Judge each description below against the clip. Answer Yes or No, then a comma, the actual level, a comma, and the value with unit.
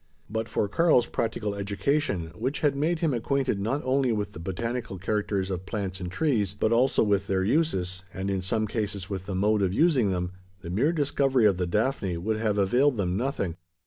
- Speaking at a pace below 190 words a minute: No, average, 200 wpm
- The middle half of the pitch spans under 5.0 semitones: No, average, 5.3 semitones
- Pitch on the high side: No, low, 105 Hz